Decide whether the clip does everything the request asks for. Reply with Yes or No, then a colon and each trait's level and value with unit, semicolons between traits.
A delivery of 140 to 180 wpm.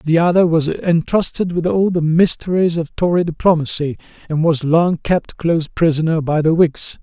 Yes: average, 170 wpm